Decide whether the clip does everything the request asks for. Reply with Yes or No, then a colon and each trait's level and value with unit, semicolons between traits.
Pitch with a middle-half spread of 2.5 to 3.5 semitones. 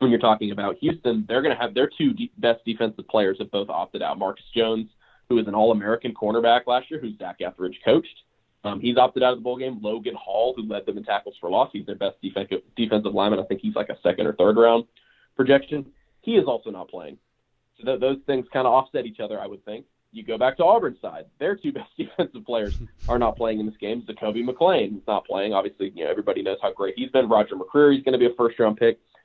Yes: average, 3.1 semitones